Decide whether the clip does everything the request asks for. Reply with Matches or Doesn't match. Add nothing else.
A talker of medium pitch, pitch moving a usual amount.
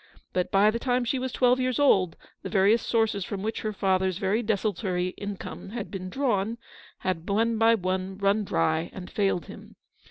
Doesn't match